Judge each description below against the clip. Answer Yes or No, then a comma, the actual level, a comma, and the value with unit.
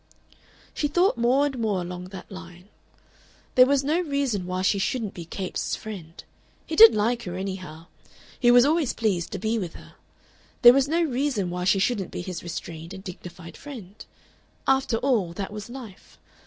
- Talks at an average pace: Yes, average, 180 wpm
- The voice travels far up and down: Yes, wide, 6.2 semitones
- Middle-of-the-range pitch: No, high, 210 Hz